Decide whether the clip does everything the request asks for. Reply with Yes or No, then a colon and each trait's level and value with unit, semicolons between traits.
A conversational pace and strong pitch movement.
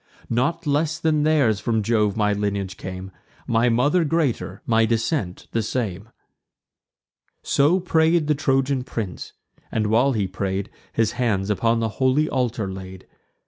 Yes: average, 145 wpm; wide, 5.7 semitones